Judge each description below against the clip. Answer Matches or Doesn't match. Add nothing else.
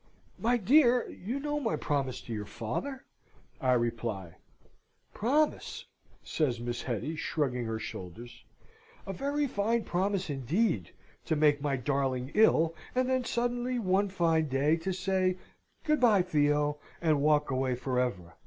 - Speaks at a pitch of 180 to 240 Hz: Doesn't match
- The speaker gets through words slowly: Doesn't match